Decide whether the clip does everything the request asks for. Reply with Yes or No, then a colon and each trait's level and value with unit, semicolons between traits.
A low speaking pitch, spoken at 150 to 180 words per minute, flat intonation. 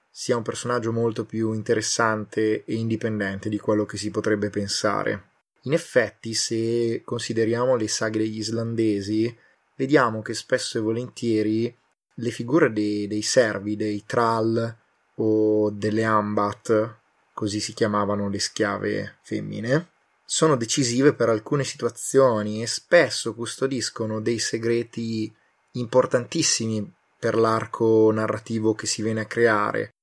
No: low, 115 Hz; average, 125 wpm; narrow, 1.5 semitones